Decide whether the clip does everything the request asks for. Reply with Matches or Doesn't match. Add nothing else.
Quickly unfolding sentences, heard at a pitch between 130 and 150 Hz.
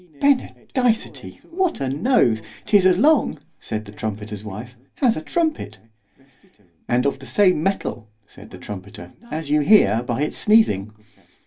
Doesn't match